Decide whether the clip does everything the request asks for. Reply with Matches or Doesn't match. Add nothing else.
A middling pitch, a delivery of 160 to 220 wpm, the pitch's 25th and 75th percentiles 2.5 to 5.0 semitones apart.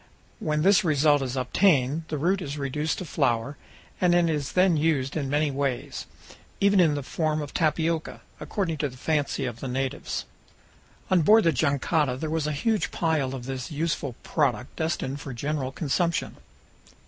Matches